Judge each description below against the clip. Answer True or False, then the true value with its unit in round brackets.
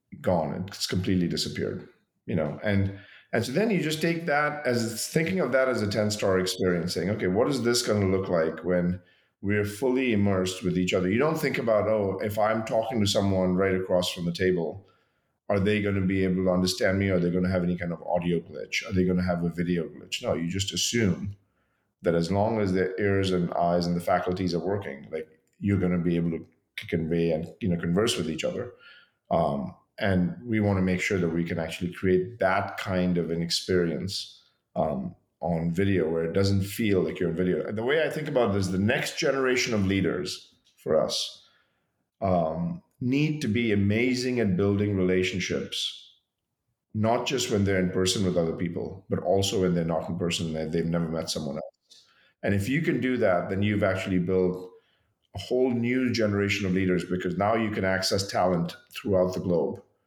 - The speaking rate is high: True (210 wpm)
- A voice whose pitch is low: True (95 Hz)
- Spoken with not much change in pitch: False (3.0 semitones)